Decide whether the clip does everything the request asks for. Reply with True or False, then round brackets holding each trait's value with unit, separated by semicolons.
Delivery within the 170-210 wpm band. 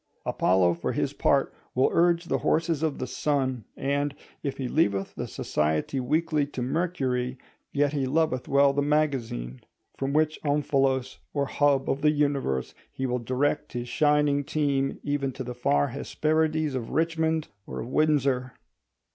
False (155 wpm)